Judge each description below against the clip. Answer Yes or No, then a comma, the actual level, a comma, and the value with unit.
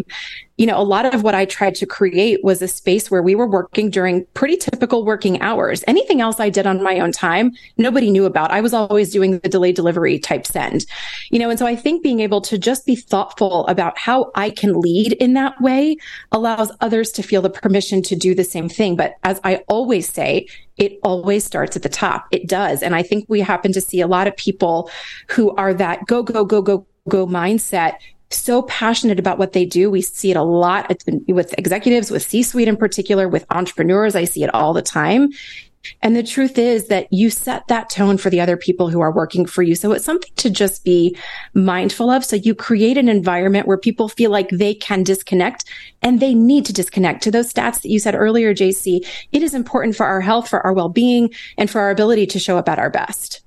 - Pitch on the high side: Yes, high, 205 Hz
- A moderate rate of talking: No, fast, 230 wpm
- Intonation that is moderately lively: Yes, average, 3.6 semitones